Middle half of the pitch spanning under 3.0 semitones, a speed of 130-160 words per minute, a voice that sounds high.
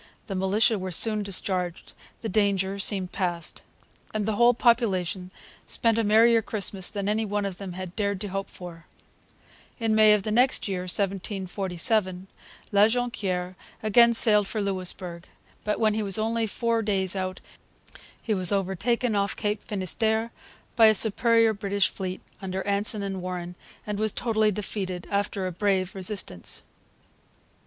Yes: narrow, 2.6 semitones; average, 155 wpm; high, 200 Hz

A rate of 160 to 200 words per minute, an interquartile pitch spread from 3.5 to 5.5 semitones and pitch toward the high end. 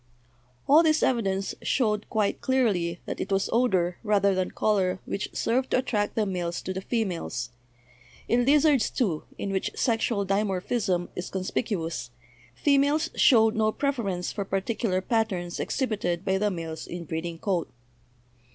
No: average, 145 wpm; average, 4.4 semitones; high, 200 Hz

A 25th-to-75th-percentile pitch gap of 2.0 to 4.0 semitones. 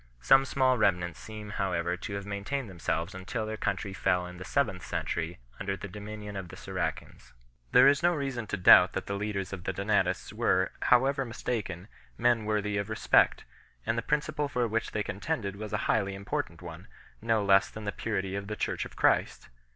Yes: average, 3.0 semitones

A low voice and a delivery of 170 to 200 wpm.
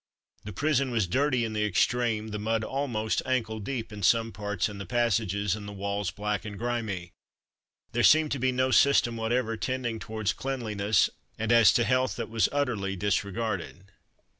Yes: low, 110 Hz; average, 175 wpm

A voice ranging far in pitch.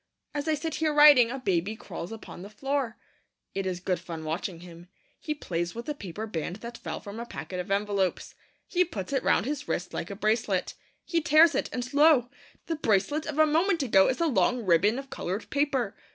Yes: wide, 7.6 semitones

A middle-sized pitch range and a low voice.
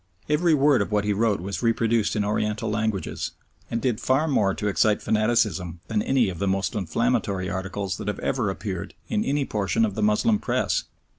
Yes: average, 3.2 semitones; low, 105 Hz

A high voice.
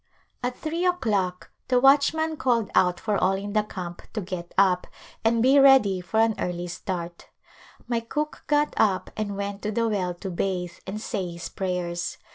Yes: high, 200 Hz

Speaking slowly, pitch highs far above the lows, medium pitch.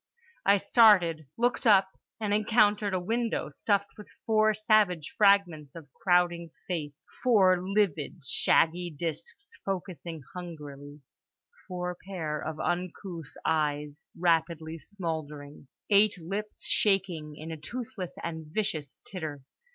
No: slow, 115 wpm; average, 4.3 semitones; medium, 175 Hz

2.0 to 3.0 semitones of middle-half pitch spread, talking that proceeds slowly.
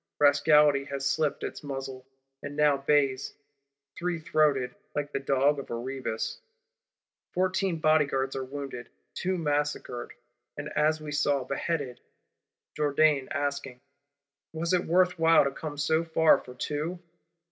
Yes: narrow, 2.4 semitones; slow, 130 wpm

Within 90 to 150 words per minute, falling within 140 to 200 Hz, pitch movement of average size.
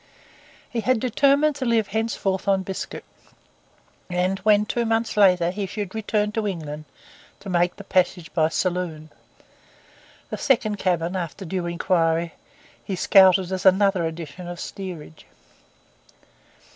Yes: slow, 135 wpm; high, 190 Hz; average, 3.3 semitones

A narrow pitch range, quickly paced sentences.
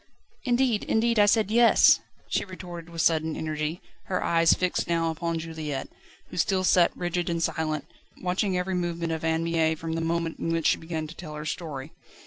No: narrow, 2.1 semitones; average, 190 wpm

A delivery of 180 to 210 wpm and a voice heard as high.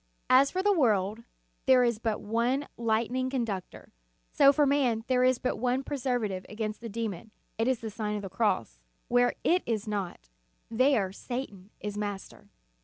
Yes: average, 185 wpm; high, 230 Hz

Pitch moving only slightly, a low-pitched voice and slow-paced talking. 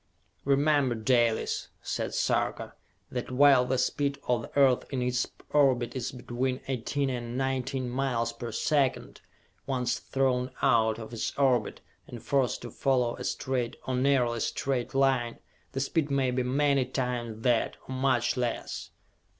No: narrow, 2.0 semitones; low, 125 Hz; average, 150 wpm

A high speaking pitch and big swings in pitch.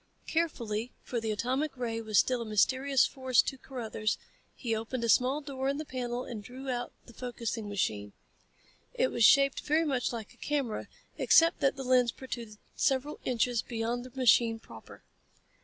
No: high, 245 Hz; average, 2.9 semitones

